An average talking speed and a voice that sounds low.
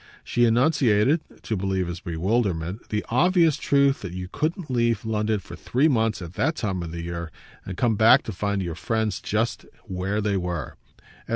Yes: average, 180 wpm; low, 105 Hz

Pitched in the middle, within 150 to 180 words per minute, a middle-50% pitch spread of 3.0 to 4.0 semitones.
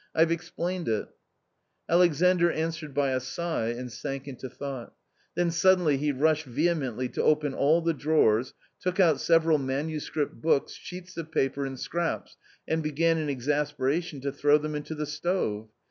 Yes: medium, 150 Hz; average, 165 wpm; average, 3.5 semitones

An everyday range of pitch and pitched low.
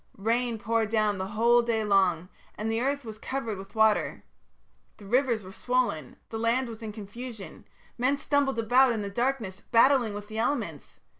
No: average, 3.0 semitones; high, 225 Hz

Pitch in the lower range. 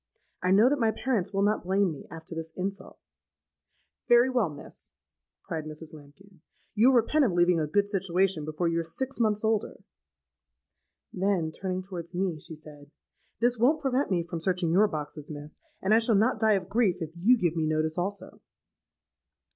No: medium, 185 Hz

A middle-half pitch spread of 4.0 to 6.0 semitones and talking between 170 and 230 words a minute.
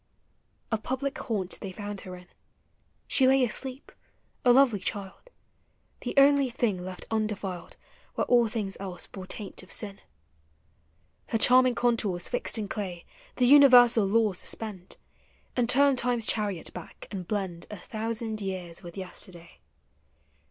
No: average, 4.5 semitones; average, 140 wpm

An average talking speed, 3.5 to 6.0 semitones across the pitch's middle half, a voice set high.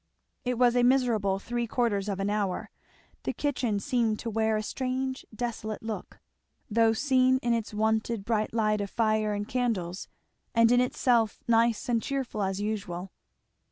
No: average, 160 wpm; average, 2.7 semitones; high, 225 Hz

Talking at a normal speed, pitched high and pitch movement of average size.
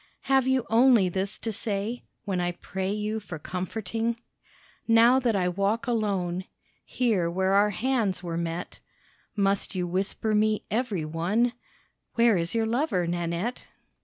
Yes: average, 145 wpm; high, 205 Hz; average, 4.1 semitones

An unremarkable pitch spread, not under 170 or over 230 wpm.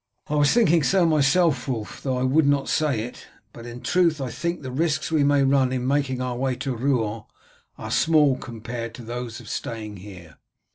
Yes: average, 3.8 semitones; average, 200 wpm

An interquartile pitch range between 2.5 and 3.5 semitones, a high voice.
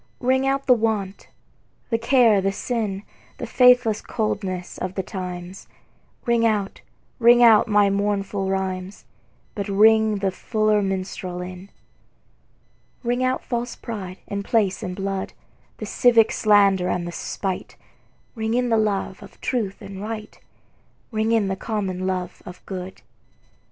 Yes: average, 3.0 semitones; high, 205 Hz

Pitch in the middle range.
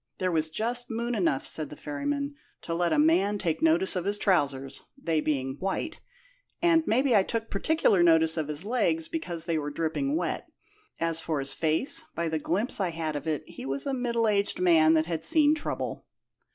Yes: medium, 170 Hz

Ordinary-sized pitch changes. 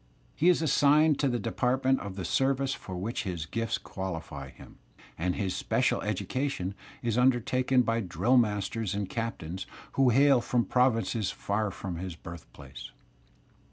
No: wide, 5.7 semitones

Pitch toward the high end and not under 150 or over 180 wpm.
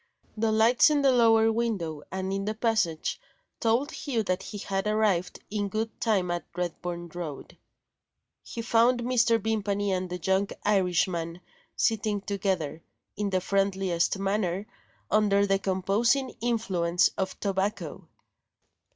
No: high, 200 Hz; slow, 135 wpm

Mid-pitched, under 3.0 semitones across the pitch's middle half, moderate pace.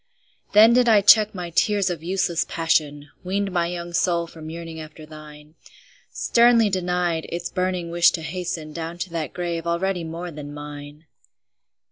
Yes: medium, 170 Hz; narrow, 2.4 semitones; average, 160 wpm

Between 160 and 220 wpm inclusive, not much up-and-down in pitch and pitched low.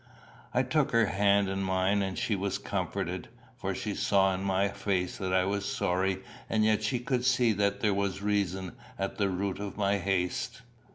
Yes: average, 190 wpm; narrow, 1.6 semitones; low, 100 Hz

